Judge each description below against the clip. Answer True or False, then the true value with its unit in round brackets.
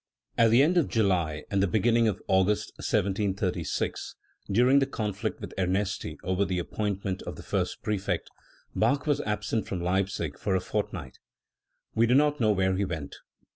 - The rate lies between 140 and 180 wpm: True (175 wpm)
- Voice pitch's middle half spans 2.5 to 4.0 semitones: True (3.3 semitones)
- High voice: False (100 Hz)